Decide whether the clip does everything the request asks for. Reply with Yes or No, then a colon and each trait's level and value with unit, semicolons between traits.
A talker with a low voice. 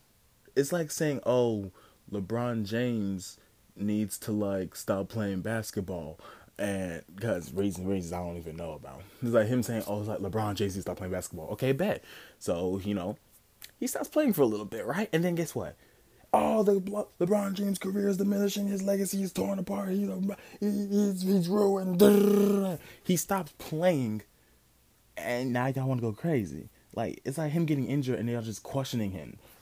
Yes: low, 125 Hz